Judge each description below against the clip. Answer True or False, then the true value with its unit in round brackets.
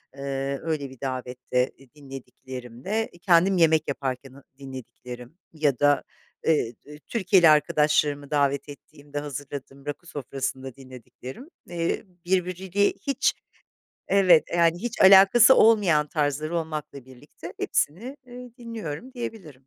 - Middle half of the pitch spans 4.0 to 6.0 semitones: True (4.9 semitones)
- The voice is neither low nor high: True (150 Hz)